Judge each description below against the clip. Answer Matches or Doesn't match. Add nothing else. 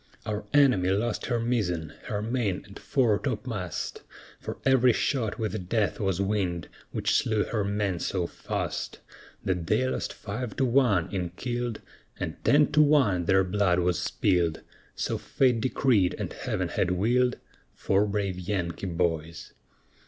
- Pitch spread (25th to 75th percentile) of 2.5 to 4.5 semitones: Doesn't match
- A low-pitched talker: Matches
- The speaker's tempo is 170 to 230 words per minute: Doesn't match